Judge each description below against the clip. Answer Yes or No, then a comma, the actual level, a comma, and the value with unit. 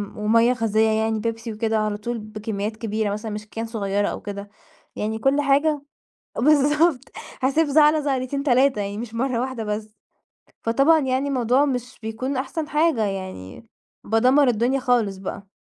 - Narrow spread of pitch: No, average, 4.2 semitones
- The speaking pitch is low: No, high, 230 Hz